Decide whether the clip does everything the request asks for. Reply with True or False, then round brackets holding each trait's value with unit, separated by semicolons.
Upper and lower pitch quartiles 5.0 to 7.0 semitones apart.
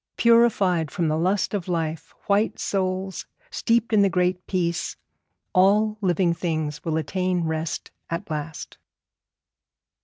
False (3.3 semitones)